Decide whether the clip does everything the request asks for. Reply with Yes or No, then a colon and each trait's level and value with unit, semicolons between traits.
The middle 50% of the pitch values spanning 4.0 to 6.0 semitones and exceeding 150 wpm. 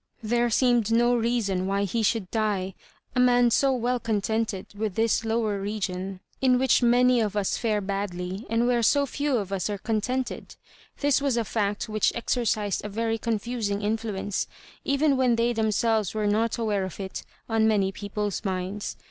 No: average, 2.9 semitones; average, 180 wpm